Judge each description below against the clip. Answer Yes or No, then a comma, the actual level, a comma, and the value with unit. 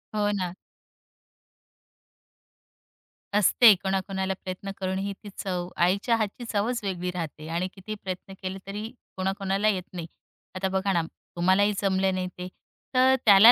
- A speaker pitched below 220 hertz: Yes, high, 190 Hz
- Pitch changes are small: Yes, narrow, 1.7 semitones